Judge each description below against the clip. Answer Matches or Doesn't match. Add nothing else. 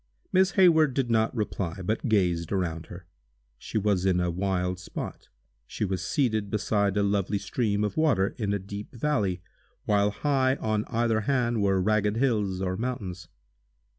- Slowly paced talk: Doesn't match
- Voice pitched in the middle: Doesn't match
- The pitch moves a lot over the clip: Doesn't match